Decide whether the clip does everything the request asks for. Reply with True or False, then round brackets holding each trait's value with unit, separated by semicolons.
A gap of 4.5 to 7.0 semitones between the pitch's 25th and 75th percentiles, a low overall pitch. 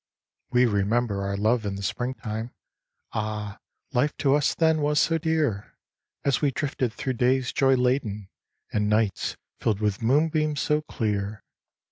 True (5.2 semitones; 120 Hz)